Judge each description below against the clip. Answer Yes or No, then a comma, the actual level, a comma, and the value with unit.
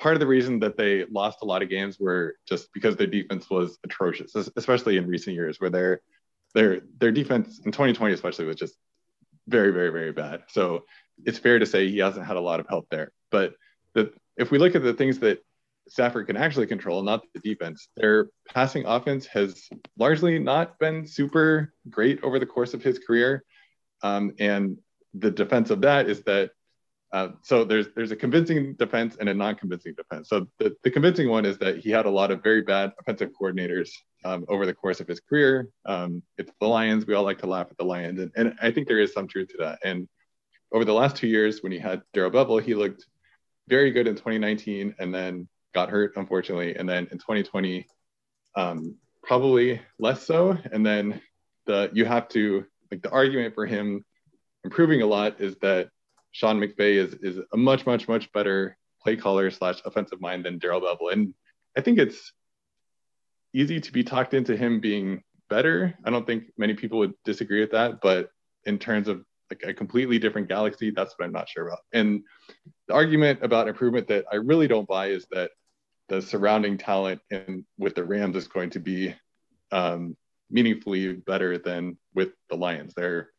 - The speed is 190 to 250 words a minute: Yes, average, 200 wpm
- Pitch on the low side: Yes, low, 105 Hz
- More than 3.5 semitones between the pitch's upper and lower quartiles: Yes, average, 4.4 semitones